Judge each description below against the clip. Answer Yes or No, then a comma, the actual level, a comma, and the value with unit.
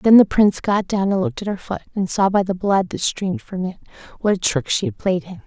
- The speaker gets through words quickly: Yes, fast, 285 wpm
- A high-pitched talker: Yes, high, 195 Hz